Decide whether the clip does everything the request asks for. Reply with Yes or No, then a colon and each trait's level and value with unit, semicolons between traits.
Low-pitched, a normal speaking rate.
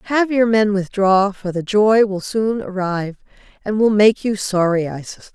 No: high, 205 Hz; average, 190 wpm